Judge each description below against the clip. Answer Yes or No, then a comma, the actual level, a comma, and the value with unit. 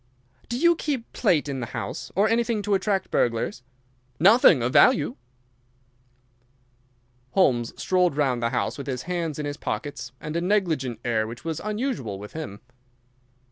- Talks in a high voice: No, medium, 155 Hz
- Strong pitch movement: Yes, wide, 8.4 semitones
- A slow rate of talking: No, average, 155 wpm